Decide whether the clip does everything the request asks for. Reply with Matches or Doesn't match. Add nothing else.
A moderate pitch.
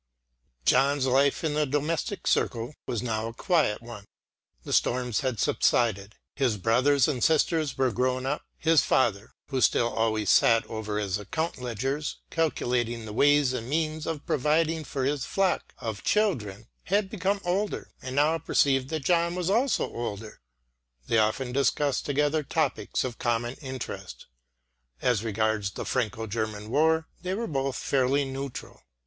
Doesn't match